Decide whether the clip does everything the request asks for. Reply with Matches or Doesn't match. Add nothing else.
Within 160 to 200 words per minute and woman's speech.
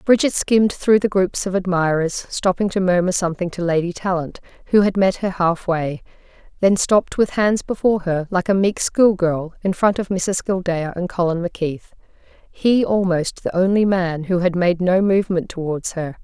Matches